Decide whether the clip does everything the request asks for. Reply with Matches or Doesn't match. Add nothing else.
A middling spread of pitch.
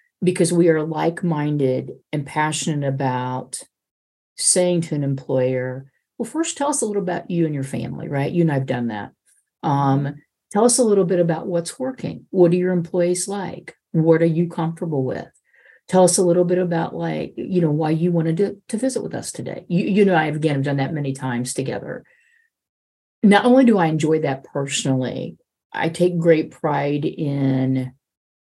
Matches